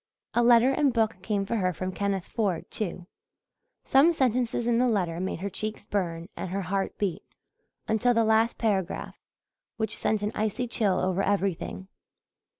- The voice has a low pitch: No, high, 210 Hz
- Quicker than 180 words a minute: No, average, 165 wpm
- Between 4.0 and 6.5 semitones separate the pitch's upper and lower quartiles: No, average, 3.5 semitones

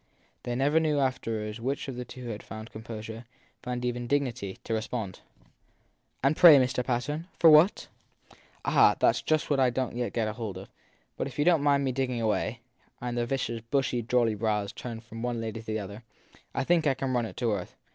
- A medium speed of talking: No, fast, 230 wpm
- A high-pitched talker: No, low, 120 Hz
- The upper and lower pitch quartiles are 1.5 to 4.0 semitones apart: Yes, average, 3.3 semitones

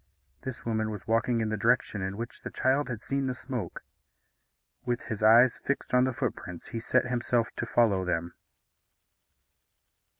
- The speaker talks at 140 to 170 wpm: Yes, average, 165 wpm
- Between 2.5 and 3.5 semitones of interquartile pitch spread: Yes, average, 3.0 semitones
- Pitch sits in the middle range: No, low, 115 Hz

